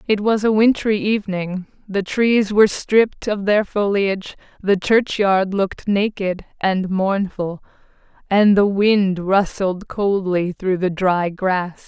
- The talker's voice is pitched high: Yes, high, 195 Hz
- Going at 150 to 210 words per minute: No, slow, 135 wpm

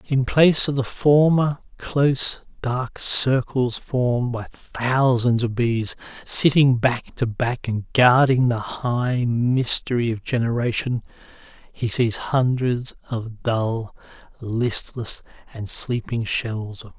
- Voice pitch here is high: No, low, 120 Hz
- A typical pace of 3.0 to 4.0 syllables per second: Yes, 3.5 syllables/s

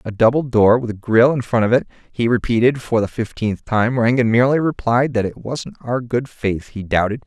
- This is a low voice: Yes, low, 115 Hz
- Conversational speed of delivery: No, fast, 225 wpm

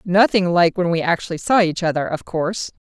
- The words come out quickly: Yes, fast, 210 wpm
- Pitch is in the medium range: Yes, medium, 175 Hz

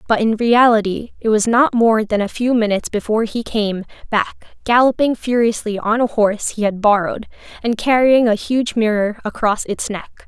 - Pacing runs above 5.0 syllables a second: Yes, 5.3 syllables/s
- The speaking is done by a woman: Yes, female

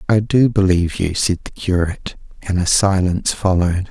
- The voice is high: No, very low, 95 Hz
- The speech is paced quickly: No, average, 170 wpm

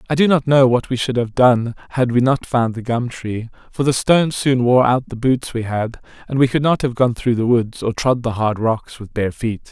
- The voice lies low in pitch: Yes, low, 125 Hz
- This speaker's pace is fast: Yes, fast, 265 wpm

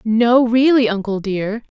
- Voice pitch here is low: No, high, 225 Hz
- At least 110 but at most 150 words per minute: Yes, slow, 135 wpm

